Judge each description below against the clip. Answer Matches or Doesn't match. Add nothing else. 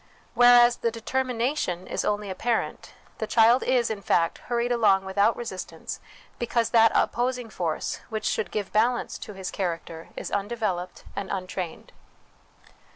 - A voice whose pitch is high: Matches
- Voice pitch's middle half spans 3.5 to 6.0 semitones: Matches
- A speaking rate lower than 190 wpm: Matches